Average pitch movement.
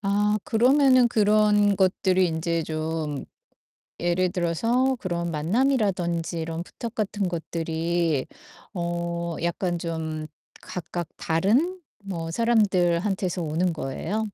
Yes: average, 4.0 semitones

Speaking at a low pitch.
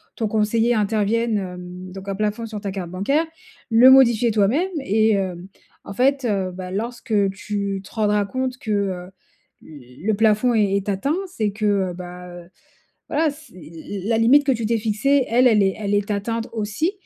No: high, 210 Hz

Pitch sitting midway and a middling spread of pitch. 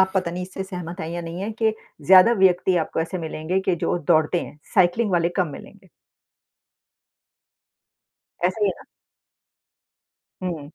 No: medium, 180 Hz; narrow, 2.1 semitones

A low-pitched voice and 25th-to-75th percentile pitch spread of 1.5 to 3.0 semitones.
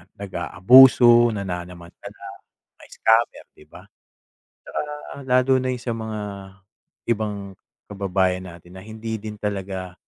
No: low, 105 Hz; average, 4.0 semitones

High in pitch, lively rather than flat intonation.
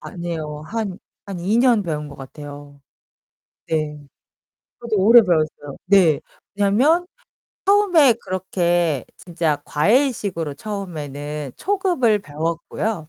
No: medium, 175 Hz; wide, 6.6 semitones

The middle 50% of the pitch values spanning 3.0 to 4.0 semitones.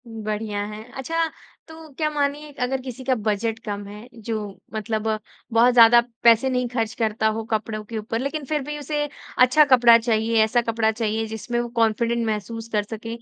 No: narrow, 2.6 semitones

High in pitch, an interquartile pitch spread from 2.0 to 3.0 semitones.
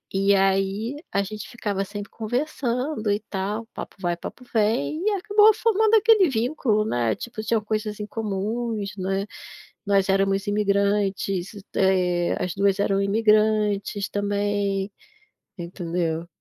Yes: high, 205 Hz; narrow, 2.4 semitones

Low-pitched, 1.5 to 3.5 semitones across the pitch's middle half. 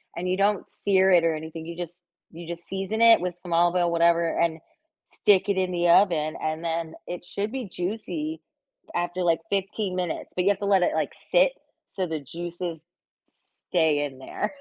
No: medium, 175 Hz; narrow, 2.6 semitones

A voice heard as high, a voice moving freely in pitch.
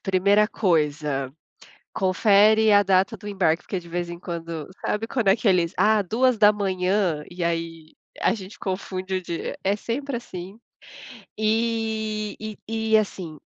No: high, 195 Hz; average, 3.7 semitones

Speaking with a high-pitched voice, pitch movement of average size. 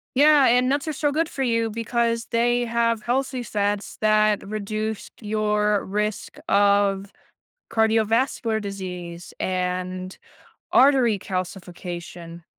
Yes: high, 215 Hz; average, 3.2 semitones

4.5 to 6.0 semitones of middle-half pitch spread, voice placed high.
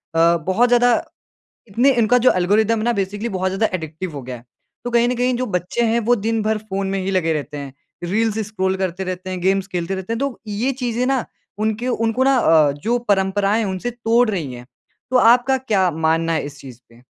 Yes: average, 5.1 semitones; high, 200 Hz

